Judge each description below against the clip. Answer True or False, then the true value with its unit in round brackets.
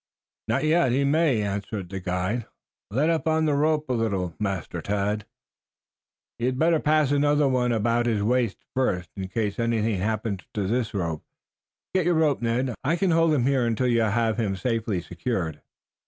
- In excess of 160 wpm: True (180 wpm)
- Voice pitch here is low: True (115 Hz)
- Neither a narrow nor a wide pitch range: False (5.7 semitones)